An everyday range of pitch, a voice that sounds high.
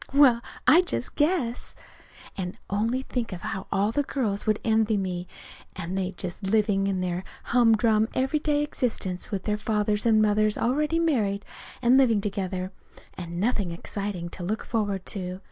Yes: average, 3.8 semitones; high, 210 Hz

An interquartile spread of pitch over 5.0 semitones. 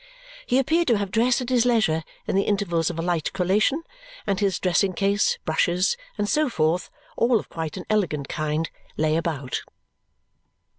Yes: wide, 5.4 semitones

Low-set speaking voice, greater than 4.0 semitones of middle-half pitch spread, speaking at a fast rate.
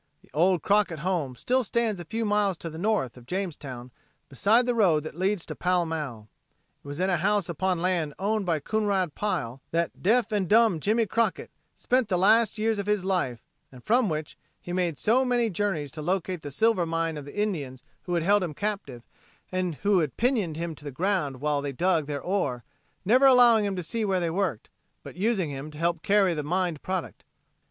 No: medium, 180 Hz; average, 5.2 semitones; fast, 210 wpm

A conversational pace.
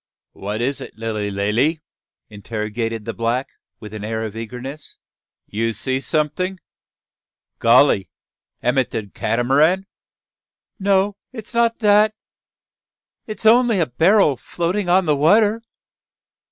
No: slow, 125 wpm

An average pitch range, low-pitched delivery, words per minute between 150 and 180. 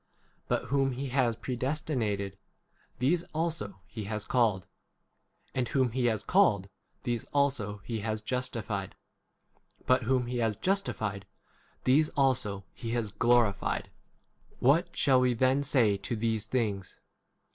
No: average, 3.9 semitones; low, 120 Hz; slow, 135 wpm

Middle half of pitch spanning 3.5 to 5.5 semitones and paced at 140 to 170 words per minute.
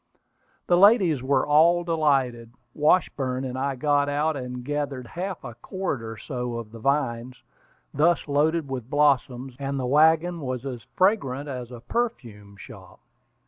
Yes: average, 4.0 semitones; average, 150 wpm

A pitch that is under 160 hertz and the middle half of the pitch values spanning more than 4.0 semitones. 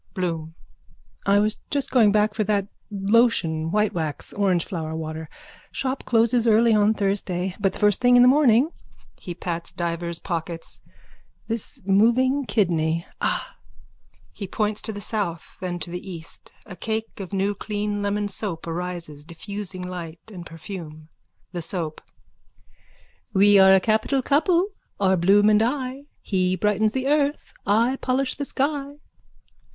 No: high, 200 Hz; average, 4.5 semitones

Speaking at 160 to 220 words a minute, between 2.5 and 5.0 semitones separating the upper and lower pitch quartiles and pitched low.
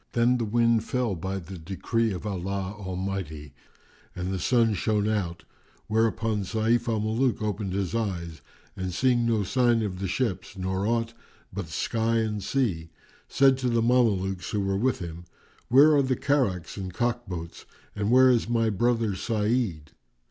Yes: average, 165 wpm; average, 3.9 semitones; low, 105 Hz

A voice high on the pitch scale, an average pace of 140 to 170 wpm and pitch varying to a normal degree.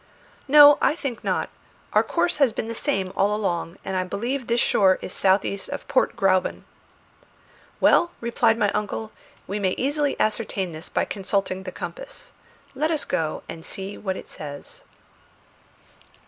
No: high, 210 Hz; average, 160 wpm; wide, 6.1 semitones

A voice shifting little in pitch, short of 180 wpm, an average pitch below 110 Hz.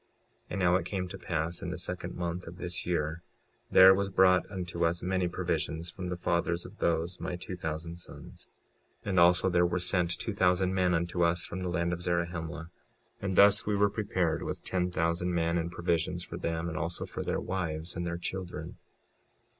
No: narrow, 1.3 semitones; fast, 205 wpm; very low, 85 Hz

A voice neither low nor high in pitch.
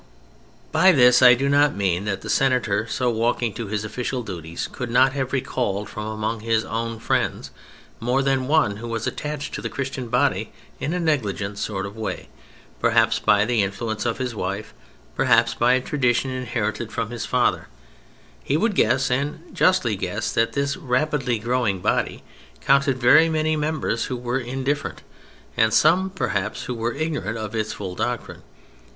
No: low, 120 Hz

